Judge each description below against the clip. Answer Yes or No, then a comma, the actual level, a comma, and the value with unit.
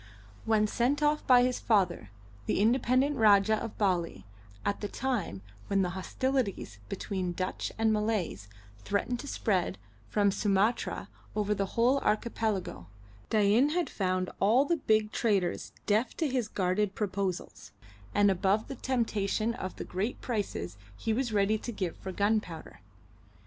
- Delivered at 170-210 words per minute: No, average, 145 wpm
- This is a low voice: No, high, 210 Hz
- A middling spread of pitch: Yes, average, 3.6 semitones